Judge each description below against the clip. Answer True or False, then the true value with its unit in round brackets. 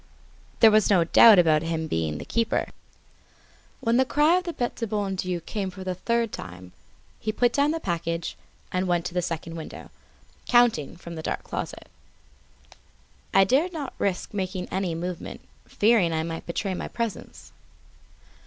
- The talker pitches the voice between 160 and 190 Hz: True (185 Hz)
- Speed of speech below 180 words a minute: True (170 wpm)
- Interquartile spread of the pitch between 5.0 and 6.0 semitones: True (5.6 semitones)